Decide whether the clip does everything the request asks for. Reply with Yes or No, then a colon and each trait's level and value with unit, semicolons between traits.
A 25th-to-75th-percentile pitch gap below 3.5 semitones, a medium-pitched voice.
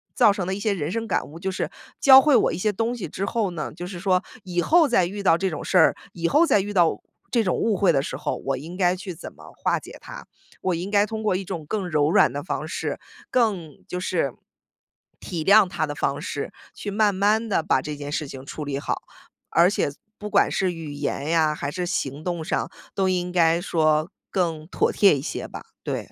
No: average, 4.3 semitones; medium, 180 Hz